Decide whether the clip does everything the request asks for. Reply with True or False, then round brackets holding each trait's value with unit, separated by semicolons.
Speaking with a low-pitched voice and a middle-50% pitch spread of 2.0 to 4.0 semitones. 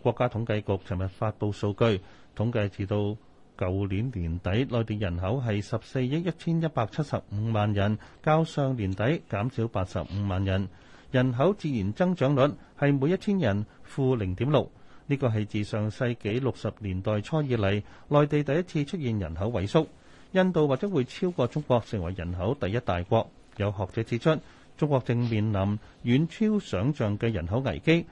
False (115 Hz; 5.1 semitones)